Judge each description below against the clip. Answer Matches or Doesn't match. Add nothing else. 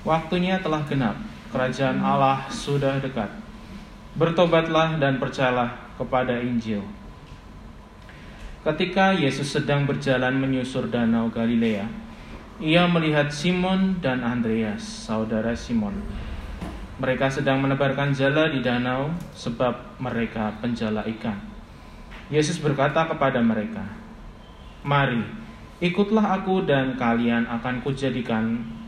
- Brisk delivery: Doesn't match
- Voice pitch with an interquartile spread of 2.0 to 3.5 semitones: Doesn't match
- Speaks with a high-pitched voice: Doesn't match